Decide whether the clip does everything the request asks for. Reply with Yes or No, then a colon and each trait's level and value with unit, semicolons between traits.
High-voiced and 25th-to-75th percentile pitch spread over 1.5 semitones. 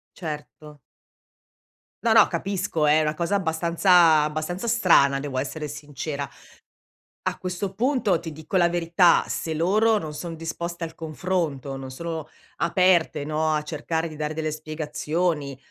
No: medium, 160 Hz; narrow, 2.6 semitones